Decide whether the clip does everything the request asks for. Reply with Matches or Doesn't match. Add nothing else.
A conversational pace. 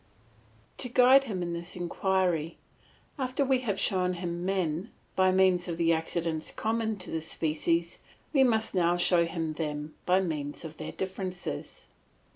Matches